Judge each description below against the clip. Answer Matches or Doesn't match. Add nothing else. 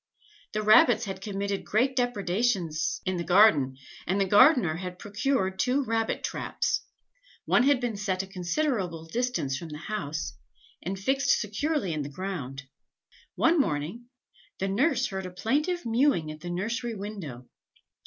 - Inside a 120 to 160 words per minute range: Matches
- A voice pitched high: Matches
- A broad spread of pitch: Matches